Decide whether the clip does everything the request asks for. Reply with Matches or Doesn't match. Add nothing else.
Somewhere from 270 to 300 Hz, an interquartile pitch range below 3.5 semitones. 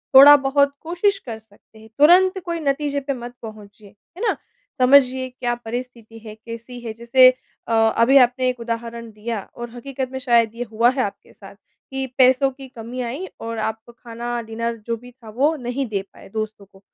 Doesn't match